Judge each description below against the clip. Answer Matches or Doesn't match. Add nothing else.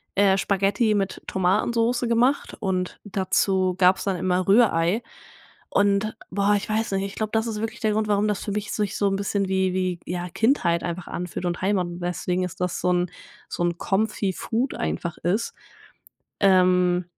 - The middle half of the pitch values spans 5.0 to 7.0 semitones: Doesn't match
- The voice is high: Matches